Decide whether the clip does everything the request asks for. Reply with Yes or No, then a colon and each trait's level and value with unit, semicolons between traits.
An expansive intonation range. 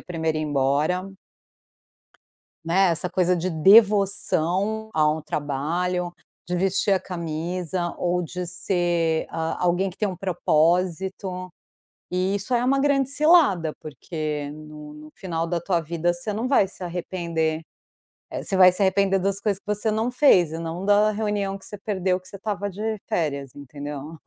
No: average, 3.4 semitones